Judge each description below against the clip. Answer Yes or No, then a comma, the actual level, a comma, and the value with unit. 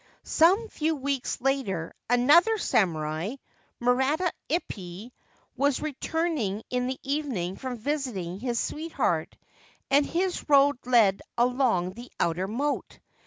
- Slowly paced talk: Yes, slow, 115 wpm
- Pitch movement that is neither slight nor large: No, wide, 6.7 semitones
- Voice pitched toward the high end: Yes, very high, 255 Hz